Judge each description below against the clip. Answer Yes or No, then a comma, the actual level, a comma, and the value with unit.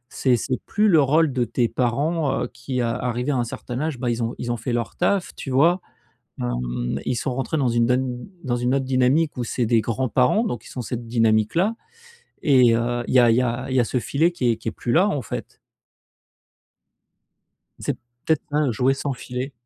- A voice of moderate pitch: No, low, 125 Hz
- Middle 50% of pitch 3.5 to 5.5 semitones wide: No, average, 2.8 semitones